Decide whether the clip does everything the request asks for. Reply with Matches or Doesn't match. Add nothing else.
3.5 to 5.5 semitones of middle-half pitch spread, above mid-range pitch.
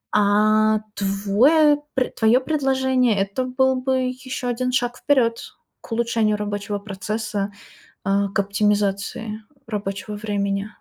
Matches